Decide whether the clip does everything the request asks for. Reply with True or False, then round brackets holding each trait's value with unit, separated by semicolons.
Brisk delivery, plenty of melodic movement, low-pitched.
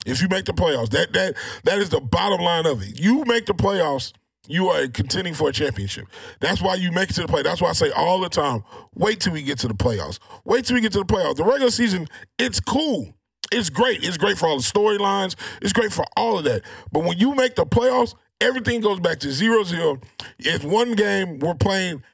False (240 wpm; 6.5 semitones; 190 Hz)